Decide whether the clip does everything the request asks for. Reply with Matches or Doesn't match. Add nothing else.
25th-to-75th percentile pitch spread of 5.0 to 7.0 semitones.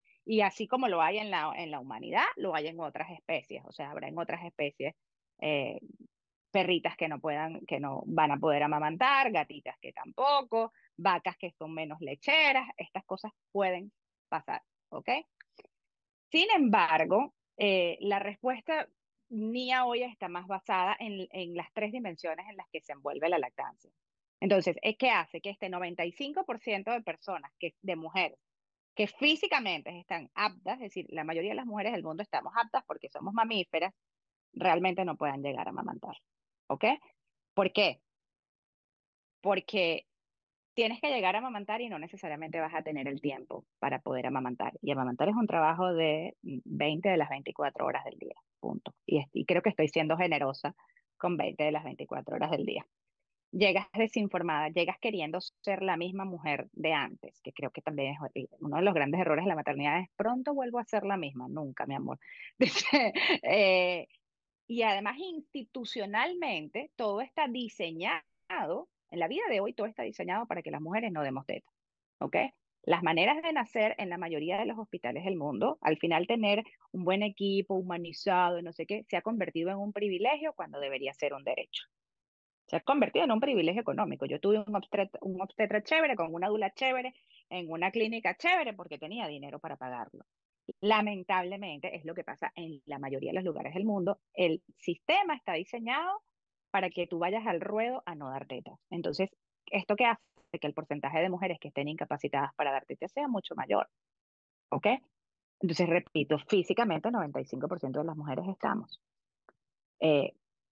Matches